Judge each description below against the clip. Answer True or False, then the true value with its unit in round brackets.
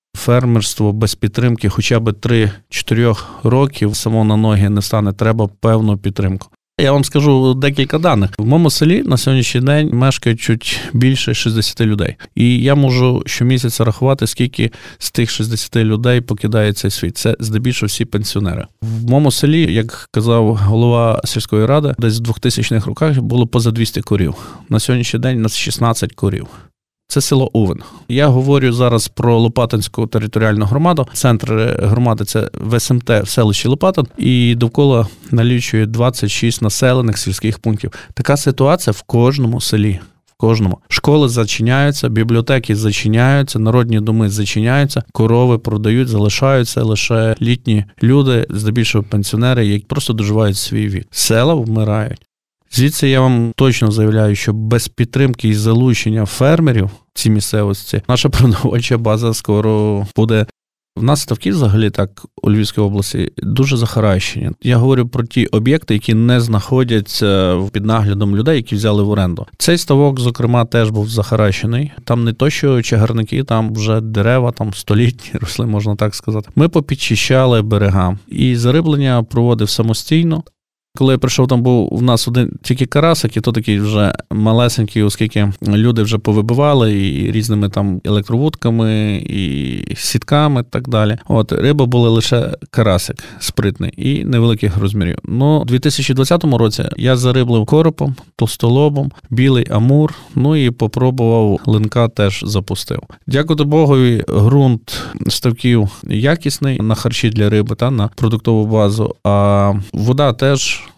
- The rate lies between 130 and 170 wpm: True (140 wpm)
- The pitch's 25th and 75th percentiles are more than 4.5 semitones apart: False (3.3 semitones)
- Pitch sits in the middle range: False (115 Hz)